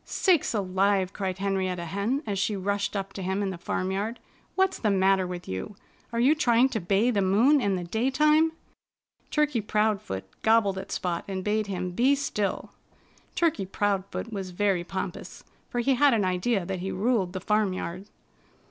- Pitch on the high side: Yes, high, 200 Hz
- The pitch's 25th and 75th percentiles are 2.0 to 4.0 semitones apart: Yes, average, 3.7 semitones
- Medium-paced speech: Yes, average, 175 wpm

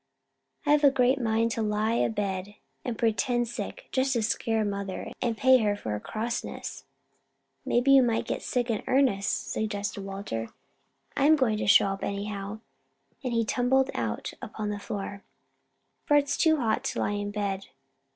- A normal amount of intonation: Yes, average, 3.5 semitones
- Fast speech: No, average, 170 wpm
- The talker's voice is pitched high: Yes, high, 220 Hz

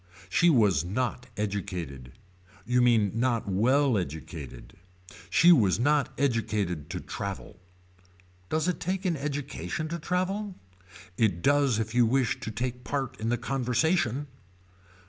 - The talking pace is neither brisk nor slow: No, slow, 130 wpm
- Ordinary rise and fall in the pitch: No, wide, 5.9 semitones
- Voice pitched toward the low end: Yes, low, 125 Hz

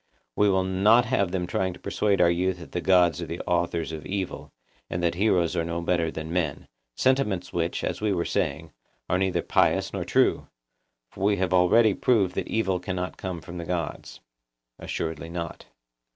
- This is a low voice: Yes, very low, 90 Hz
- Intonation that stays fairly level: Yes, narrow, 2.1 semitones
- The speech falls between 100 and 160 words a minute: No, average, 185 wpm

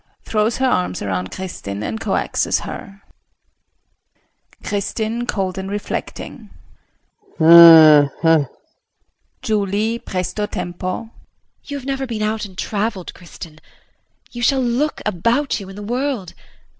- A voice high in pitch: Yes, high, 200 Hz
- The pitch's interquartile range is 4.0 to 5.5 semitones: Yes, average, 5.1 semitones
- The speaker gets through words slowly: Yes, slow, 120 wpm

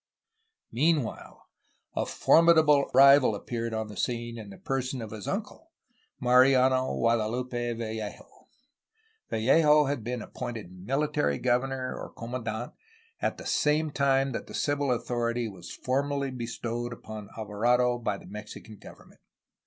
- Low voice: Yes, low, 120 Hz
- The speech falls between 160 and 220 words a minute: No, slow, 135 wpm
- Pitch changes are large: No, average, 3.3 semitones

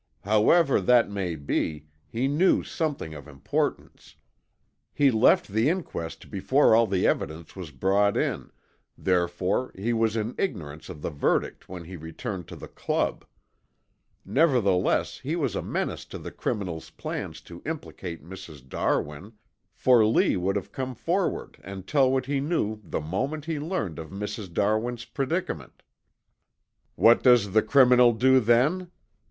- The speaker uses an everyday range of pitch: No, wide, 6.9 semitones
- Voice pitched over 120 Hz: No, low, 105 Hz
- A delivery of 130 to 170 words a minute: Yes, average, 145 wpm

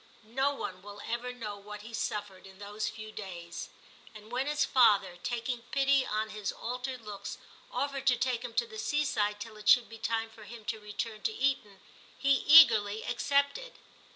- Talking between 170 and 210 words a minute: Yes, average, 180 wpm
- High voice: Yes, high, 225 Hz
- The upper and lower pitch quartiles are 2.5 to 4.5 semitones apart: Yes, average, 4.2 semitones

